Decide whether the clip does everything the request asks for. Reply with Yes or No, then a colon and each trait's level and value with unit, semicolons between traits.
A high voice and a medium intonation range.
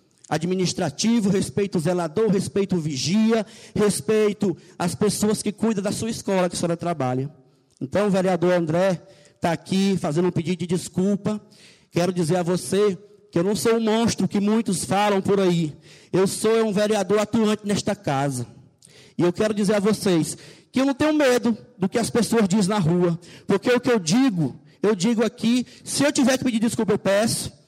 Yes: high, 195 Hz; average, 3.6 semitones